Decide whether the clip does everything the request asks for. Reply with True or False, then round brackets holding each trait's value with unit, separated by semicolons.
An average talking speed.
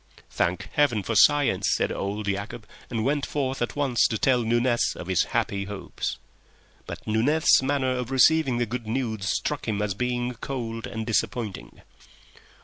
True (160 wpm)